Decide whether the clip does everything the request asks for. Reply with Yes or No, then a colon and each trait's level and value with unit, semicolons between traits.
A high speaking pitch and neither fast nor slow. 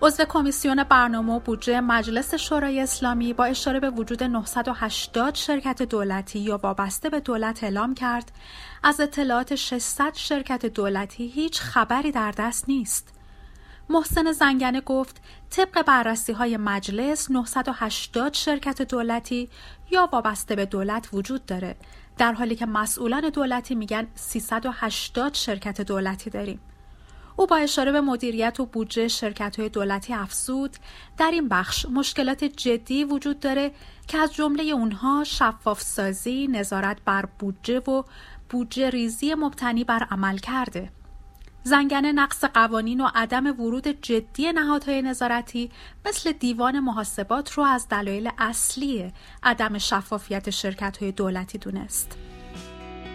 Yes: high, 240 Hz; average, 130 wpm